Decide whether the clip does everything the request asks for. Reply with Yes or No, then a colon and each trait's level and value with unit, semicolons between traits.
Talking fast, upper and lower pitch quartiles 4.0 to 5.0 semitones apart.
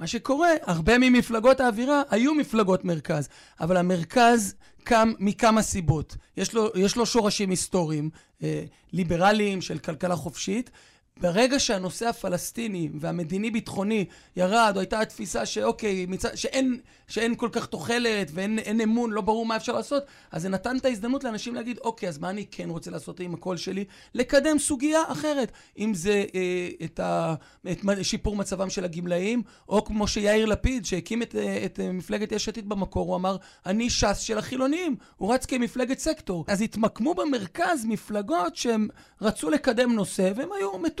Yes: fast, 160 wpm; average, 4.6 semitones